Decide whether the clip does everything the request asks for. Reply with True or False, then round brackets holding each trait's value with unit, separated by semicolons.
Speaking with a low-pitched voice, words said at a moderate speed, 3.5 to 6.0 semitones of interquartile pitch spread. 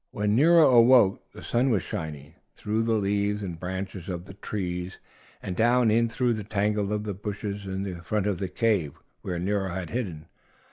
False (100 Hz; 180 wpm; 3.0 semitones)